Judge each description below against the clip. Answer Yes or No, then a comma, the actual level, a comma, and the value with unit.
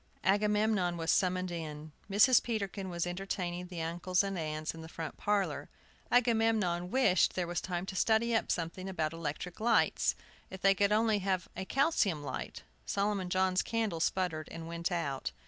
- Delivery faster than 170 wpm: No, average, 165 wpm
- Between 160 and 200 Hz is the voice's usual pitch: Yes, medium, 185 Hz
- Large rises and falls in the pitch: No, average, 3.5 semitones